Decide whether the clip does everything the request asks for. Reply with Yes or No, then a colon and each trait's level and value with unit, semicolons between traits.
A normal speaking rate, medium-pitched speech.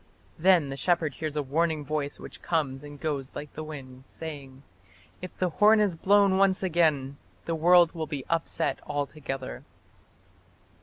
Yes: average, 155 wpm; medium, 155 Hz